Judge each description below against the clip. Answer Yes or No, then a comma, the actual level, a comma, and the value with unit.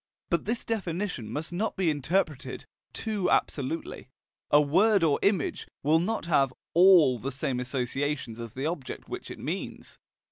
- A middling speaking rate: Yes, average, 150 wpm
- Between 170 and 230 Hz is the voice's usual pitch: No, medium, 155 Hz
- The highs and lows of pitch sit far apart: Yes, wide, 5.8 semitones